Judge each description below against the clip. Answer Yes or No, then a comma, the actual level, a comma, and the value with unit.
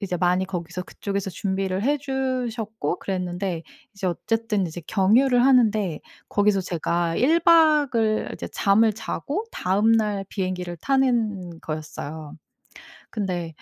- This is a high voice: Yes, high, 200 Hz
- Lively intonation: No, average, 4.3 semitones